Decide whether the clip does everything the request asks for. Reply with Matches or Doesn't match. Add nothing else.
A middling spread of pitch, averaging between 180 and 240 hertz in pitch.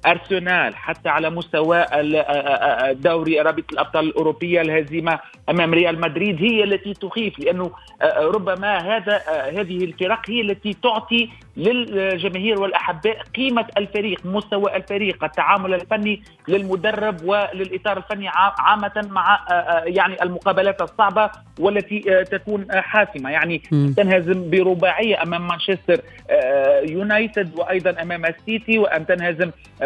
Matches